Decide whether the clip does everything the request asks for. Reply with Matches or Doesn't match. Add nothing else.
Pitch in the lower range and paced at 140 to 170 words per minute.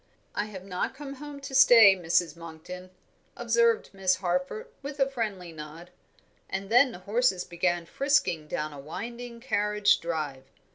Doesn't match